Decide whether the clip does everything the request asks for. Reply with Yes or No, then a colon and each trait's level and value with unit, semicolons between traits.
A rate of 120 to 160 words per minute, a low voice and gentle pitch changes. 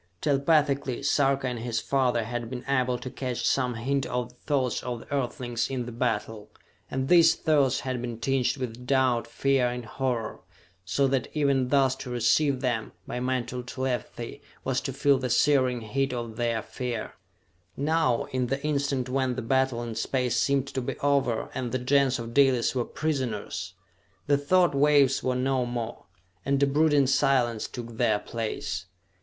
No: average, 170 wpm; low, 130 Hz; narrow, 2.3 semitones